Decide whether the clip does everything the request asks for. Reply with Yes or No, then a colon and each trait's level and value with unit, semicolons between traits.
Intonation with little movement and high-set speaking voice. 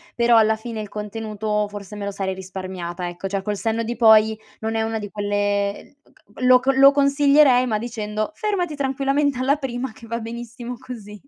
No: average, 3.6 semitones; high, 225 Hz